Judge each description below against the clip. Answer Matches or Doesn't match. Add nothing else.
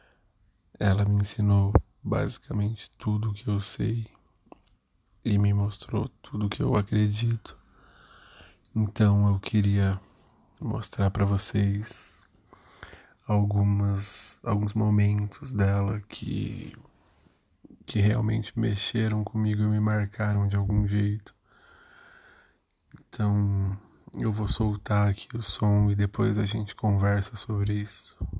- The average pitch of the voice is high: Doesn't match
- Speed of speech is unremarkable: Doesn't match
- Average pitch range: Doesn't match